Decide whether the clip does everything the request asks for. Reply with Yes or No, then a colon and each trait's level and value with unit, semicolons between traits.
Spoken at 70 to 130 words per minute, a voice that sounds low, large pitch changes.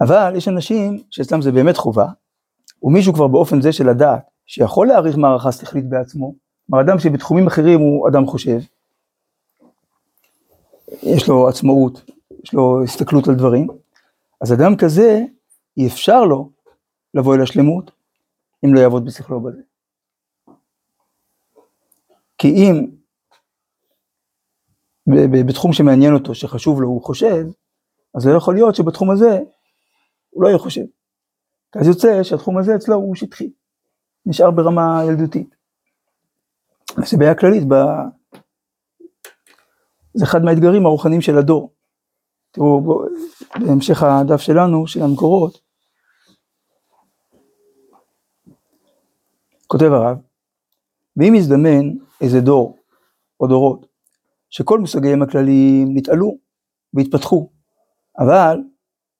No: average, 110 wpm; medium, 155 Hz; wide, 5.8 semitones